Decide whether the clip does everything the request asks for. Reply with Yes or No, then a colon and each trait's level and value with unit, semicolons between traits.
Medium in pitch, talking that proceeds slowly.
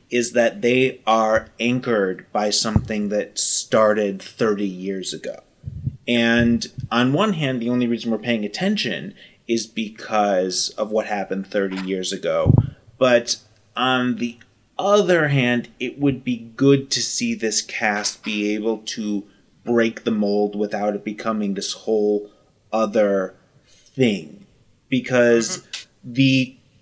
No: low, 115 Hz; slow, 130 wpm